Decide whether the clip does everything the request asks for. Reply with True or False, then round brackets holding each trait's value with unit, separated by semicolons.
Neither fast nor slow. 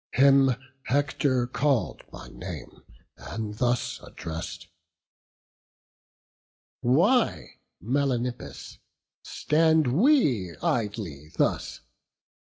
False (65 wpm)